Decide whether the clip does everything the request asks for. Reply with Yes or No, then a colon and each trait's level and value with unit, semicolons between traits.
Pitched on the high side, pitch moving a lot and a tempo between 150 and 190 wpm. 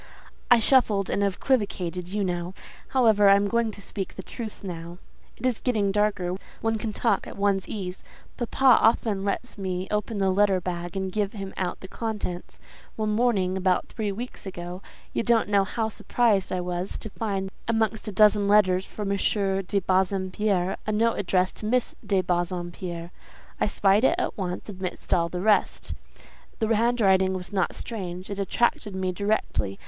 No: high, 200 Hz; average, 2.8 semitones; average, 175 wpm